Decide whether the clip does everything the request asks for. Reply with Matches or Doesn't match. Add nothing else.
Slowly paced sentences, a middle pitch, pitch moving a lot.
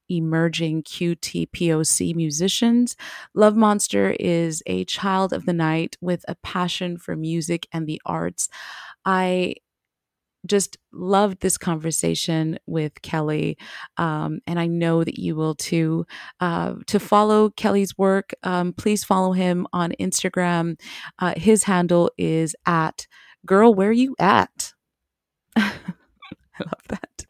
Doesn't match